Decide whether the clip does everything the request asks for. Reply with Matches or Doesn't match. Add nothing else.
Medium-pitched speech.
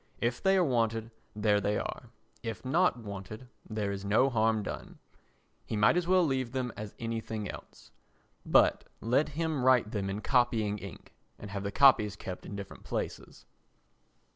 Doesn't match